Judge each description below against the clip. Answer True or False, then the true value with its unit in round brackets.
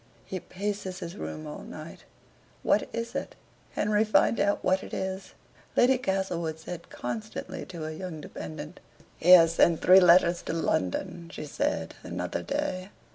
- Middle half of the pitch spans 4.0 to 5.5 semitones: False (3.4 semitones)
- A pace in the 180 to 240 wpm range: False (155 wpm)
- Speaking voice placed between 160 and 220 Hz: True (185 Hz)